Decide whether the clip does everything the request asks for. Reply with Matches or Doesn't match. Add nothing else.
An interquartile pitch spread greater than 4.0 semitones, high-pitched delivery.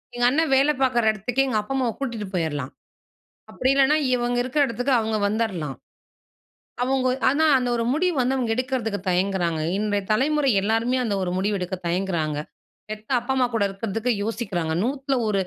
Matches